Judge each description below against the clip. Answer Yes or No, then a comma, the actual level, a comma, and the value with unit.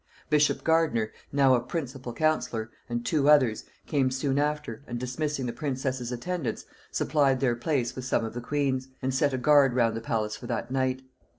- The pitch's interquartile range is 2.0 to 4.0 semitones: Yes, average, 3.3 semitones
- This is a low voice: Yes, low, 130 Hz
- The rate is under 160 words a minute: No, average, 185 wpm